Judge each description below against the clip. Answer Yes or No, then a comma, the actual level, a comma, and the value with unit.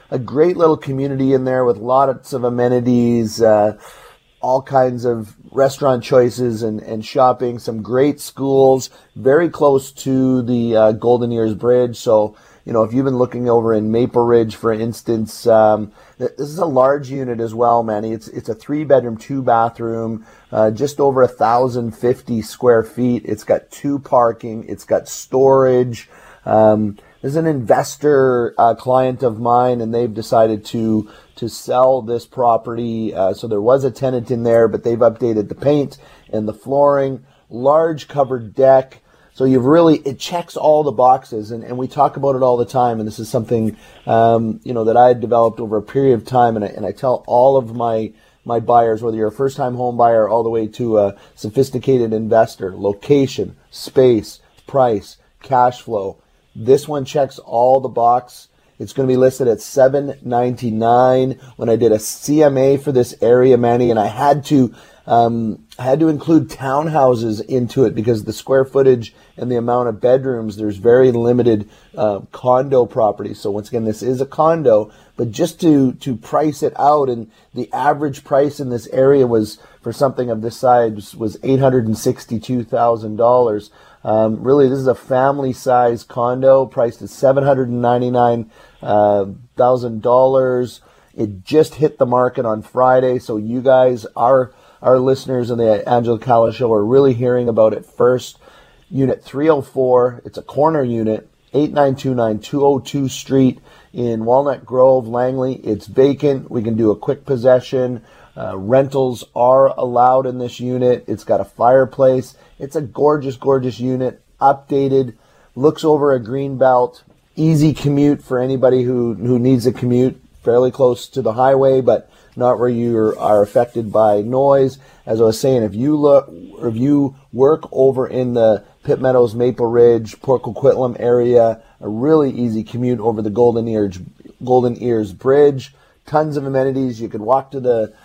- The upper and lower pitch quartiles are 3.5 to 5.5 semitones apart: No, average, 2.7 semitones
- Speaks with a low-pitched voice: Yes, low, 125 Hz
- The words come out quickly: No, average, 170 wpm